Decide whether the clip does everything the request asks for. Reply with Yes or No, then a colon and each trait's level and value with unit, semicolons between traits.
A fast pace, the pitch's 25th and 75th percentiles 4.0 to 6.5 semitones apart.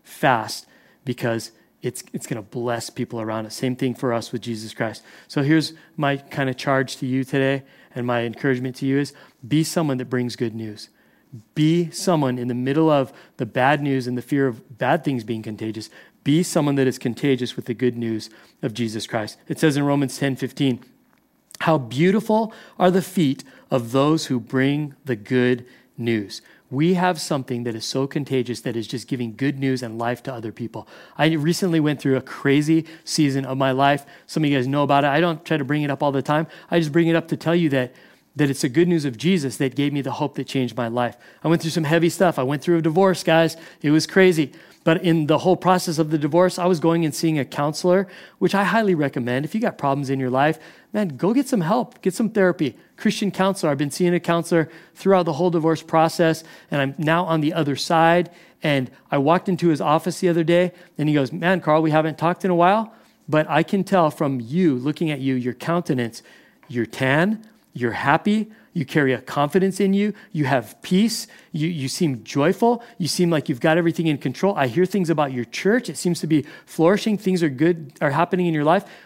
Yes: fast, 225 wpm; average, 4.5 semitones